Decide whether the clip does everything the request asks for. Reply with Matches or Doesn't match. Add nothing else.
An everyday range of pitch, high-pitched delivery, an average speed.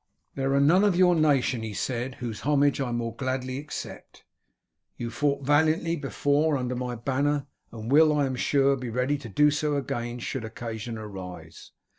Doesn't match